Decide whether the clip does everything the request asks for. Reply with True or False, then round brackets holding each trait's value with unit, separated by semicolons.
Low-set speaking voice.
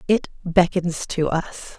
False (175 Hz)